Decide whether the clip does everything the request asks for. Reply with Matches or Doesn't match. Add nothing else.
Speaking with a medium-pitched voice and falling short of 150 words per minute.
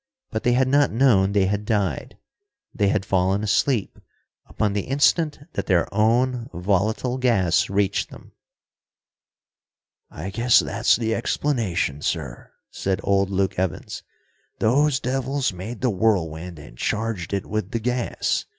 Doesn't match